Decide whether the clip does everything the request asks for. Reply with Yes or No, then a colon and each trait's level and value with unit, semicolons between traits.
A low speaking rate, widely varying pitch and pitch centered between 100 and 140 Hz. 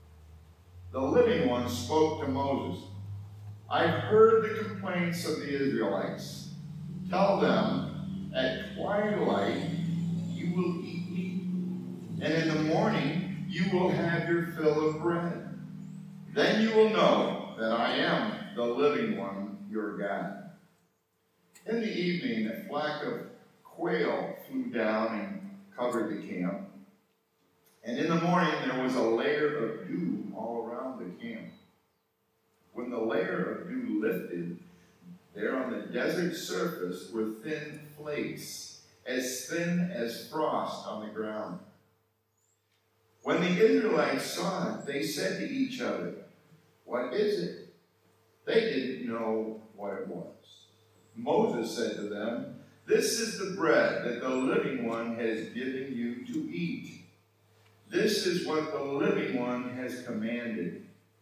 No: slow, 130 wpm; wide, 8.3 semitones; medium, 150 Hz